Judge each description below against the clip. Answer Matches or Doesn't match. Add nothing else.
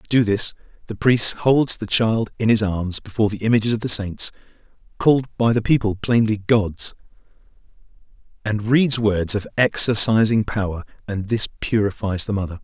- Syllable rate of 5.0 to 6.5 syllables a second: Doesn't match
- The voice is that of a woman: Doesn't match